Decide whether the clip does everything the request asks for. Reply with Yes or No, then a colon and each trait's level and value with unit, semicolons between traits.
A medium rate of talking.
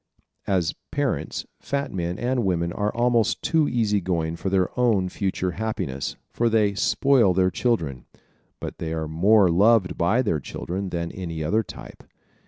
Yes: average, 160 wpm